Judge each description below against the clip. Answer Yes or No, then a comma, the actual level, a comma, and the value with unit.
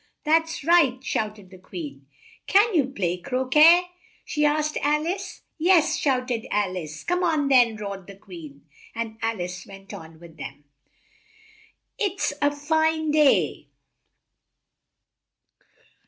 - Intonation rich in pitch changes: Yes, wide, 8.5 semitones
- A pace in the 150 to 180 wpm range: No, slow, 135 wpm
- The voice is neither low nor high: No, very high, 260 Hz